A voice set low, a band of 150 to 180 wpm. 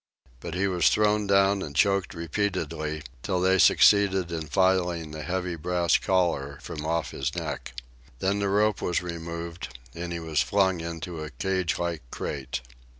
Yes: very low, 85 Hz; average, 155 wpm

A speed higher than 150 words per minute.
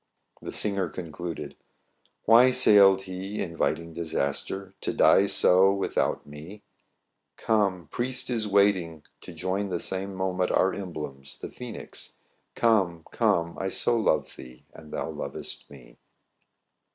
No: average, 140 wpm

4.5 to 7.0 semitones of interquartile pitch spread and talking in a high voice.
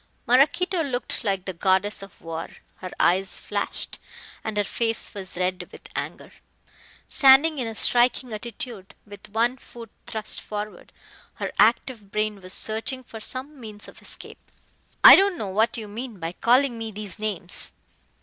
No: average, 3.8 semitones; high, 220 Hz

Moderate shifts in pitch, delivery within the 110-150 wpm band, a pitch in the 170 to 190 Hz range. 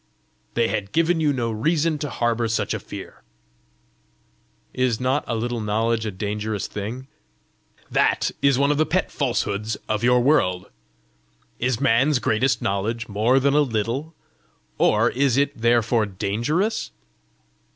No: average, 4.4 semitones; average, 140 wpm; low, 120 Hz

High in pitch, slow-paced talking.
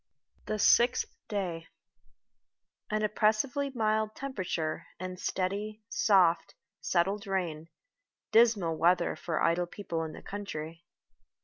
Yes: high, 195 Hz; slow, 105 wpm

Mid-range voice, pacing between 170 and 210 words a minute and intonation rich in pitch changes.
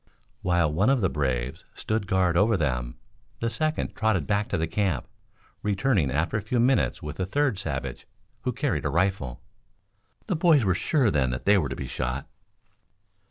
No: very low, 95 Hz; average, 180 wpm; wide, 6.7 semitones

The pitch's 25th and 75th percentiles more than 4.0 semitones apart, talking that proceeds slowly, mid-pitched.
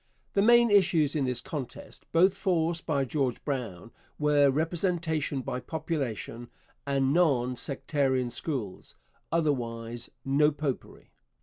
Yes: average, 4.4 semitones; slow, 115 wpm; medium, 145 Hz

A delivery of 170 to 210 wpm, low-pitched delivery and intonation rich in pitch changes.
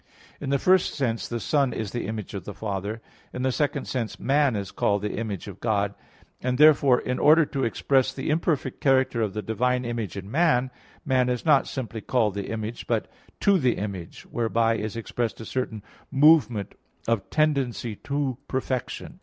No: average, 185 wpm; low, 120 Hz; average, 4.0 semitones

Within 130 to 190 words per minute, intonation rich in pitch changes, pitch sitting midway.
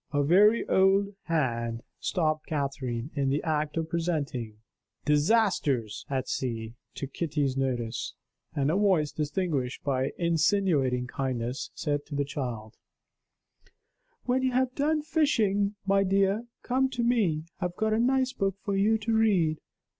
Yes: average, 145 wpm; wide, 7.1 semitones; medium, 160 Hz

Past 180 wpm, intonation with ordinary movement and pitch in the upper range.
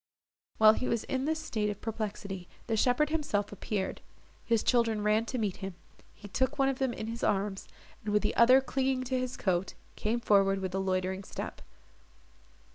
Yes: average, 190 wpm; average, 4.2 semitones; high, 215 Hz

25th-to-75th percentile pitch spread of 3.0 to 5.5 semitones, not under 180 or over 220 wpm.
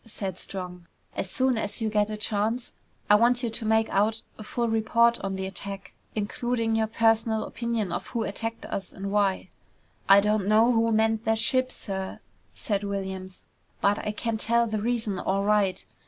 No: narrow, 2.4 semitones; average, 185 wpm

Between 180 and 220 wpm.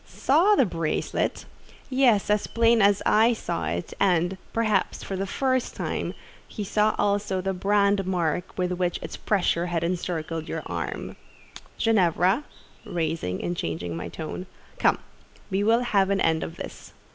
No: average, 155 wpm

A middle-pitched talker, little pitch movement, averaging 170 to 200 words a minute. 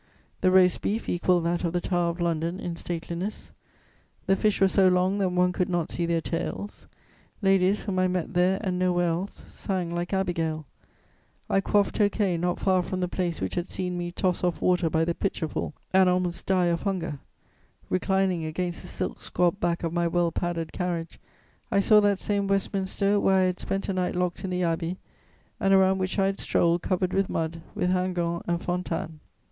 Yes: medium, 180 Hz; narrow, 1.8 semitones; average, 195 wpm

